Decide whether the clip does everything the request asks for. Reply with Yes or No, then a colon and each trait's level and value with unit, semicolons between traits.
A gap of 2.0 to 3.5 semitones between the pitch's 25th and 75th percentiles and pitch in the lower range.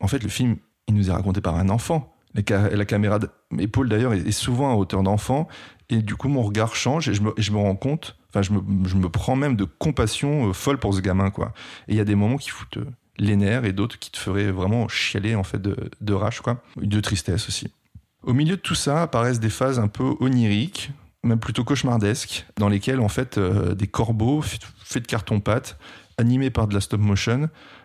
No: average, 3.9 semitones; low, 110 Hz